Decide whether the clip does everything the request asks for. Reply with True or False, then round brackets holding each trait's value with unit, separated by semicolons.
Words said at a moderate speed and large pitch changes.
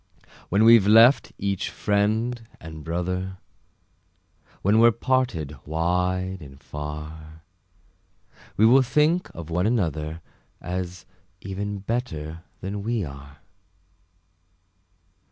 False (100 wpm; 5.8 semitones)